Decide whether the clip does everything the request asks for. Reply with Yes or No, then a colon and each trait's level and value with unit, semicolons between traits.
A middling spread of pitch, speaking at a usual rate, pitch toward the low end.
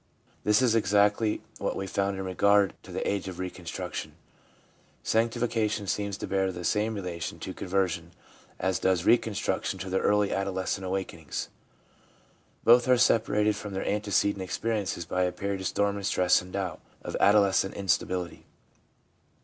No: narrow, 2.1 semitones; average, 160 wpm; low, 100 Hz